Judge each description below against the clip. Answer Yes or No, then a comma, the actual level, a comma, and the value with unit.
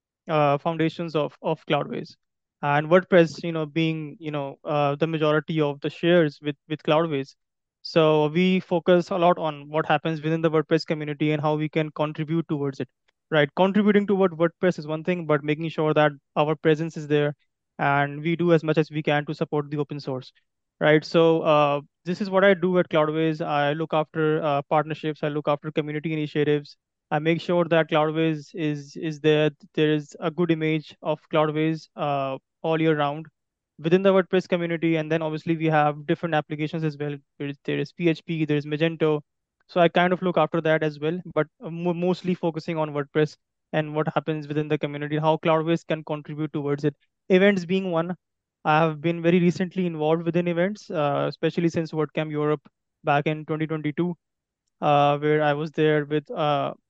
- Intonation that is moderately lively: No, narrow, 1.9 semitones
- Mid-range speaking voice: Yes, medium, 155 Hz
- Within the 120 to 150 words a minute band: No, average, 190 wpm